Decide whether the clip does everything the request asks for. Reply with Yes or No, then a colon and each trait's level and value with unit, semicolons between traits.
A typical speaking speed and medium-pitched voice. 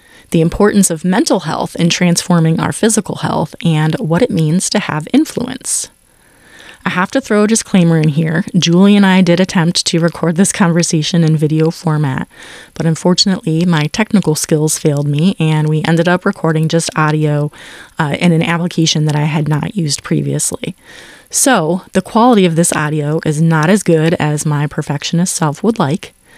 Yes: average, 175 wpm; medium, 165 Hz